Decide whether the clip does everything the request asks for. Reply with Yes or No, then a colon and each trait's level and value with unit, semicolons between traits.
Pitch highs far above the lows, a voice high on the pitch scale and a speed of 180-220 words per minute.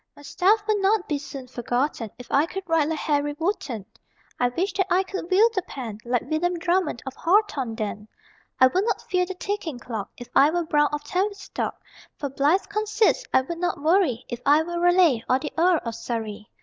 Yes: wide, 6.4 semitones; very high, 315 Hz; average, 200 wpm